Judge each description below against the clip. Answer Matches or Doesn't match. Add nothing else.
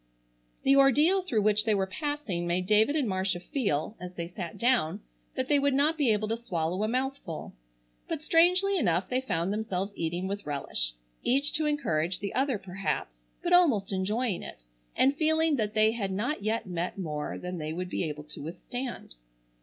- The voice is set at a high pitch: Matches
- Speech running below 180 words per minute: Doesn't match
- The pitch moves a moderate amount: Doesn't match